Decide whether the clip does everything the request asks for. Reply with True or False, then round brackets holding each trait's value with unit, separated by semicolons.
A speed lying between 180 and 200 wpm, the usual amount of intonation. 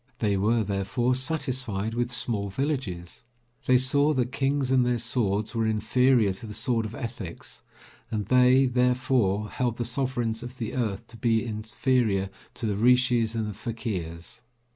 False (160 wpm; 3.1 semitones)